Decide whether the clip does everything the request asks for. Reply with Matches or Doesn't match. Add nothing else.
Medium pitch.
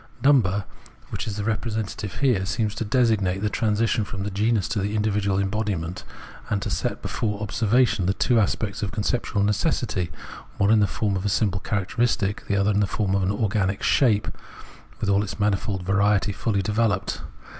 Doesn't match